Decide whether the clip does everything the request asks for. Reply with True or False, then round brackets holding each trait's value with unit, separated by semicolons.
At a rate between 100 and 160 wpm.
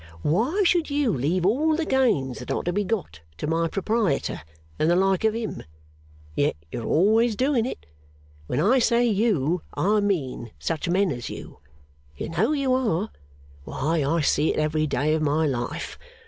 False (175 wpm)